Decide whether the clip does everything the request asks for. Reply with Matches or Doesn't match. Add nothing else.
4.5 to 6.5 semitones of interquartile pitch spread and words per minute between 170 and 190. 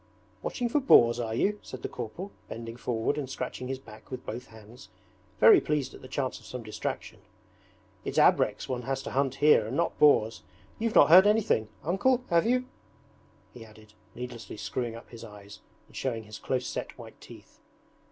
Matches